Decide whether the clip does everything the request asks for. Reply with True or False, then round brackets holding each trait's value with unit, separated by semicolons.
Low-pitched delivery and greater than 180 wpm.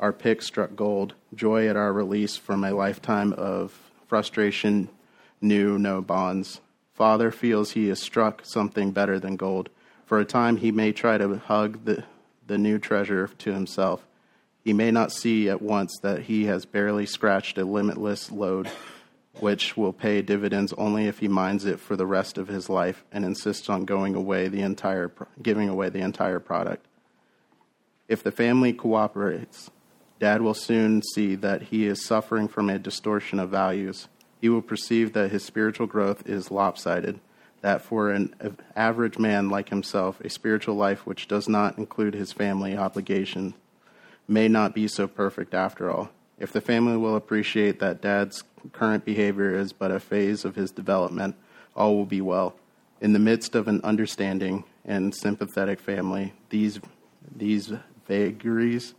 False (100 Hz; 165 wpm)